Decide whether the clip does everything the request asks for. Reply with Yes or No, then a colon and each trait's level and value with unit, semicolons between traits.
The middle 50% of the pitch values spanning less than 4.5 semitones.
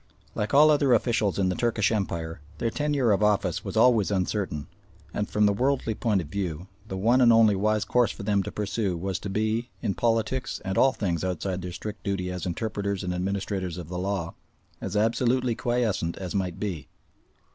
Yes: average, 3.6 semitones